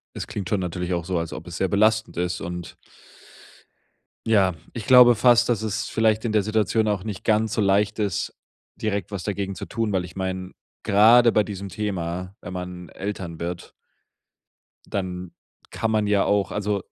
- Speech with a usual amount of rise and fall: Yes, average, 3.1 semitones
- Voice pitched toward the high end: No, low, 100 Hz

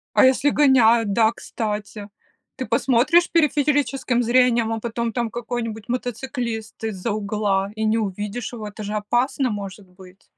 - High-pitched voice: Yes, high, 225 Hz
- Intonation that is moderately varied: Yes, average, 3.0 semitones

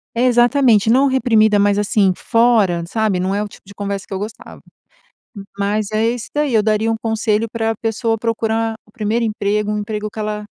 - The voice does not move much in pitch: Yes, narrow, 1.7 semitones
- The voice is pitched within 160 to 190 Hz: No, high, 215 Hz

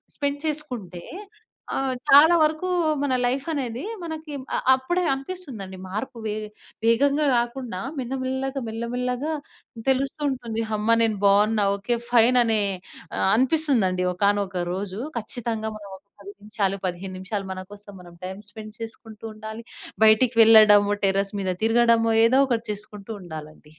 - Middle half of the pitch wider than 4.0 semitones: Yes, average, 4.4 semitones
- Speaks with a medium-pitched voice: No, high, 225 Hz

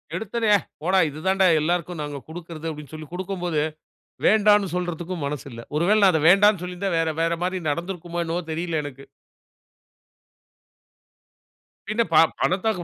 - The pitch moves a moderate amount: Yes, average, 3.3 semitones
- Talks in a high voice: No, medium, 175 Hz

